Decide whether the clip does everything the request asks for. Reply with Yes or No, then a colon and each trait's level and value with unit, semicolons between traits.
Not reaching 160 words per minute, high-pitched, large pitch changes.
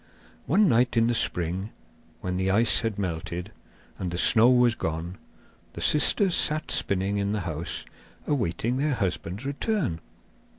No: average, 145 wpm; low, 105 Hz; wide, 5.9 semitones